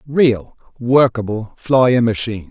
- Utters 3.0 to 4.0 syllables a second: Yes, 3.8 syllables/s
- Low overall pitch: Yes, low, 120 Hz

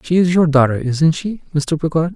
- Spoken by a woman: No, male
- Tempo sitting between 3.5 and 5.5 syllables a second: No, 5.7 syllables/s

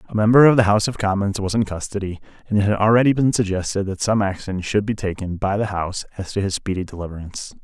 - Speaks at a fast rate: Yes, fast, 235 wpm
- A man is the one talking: Yes, male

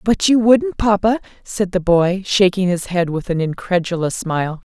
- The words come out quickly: No, average, 180 wpm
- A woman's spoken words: Yes, female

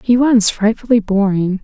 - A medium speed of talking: Yes, average, 145 wpm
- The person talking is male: No, female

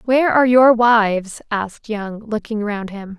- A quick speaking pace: No, average, 170 wpm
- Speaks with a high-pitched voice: Yes, high, 220 Hz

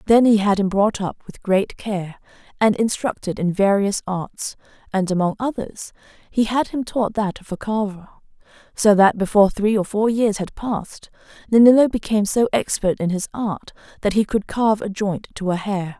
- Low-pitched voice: No, high, 205 Hz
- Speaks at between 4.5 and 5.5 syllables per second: Yes, 5.0 syllables/s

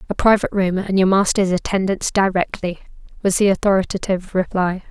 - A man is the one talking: No, female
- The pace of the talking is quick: No, average, 145 wpm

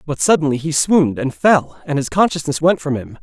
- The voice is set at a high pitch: No, medium, 150 Hz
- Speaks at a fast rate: Yes, fast, 225 wpm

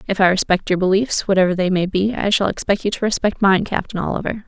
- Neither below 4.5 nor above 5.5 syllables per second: No, 6.3 syllables/s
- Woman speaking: Yes, female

